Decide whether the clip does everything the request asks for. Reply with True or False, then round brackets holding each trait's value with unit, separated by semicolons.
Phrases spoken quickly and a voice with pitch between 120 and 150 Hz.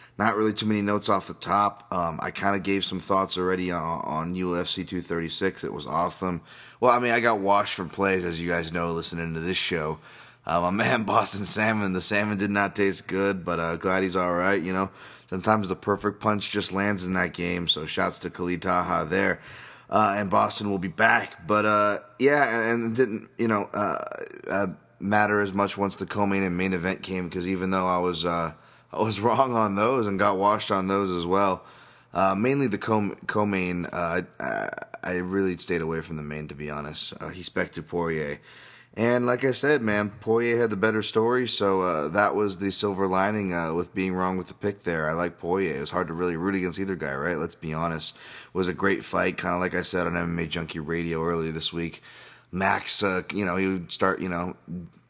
False (220 wpm; 95 Hz)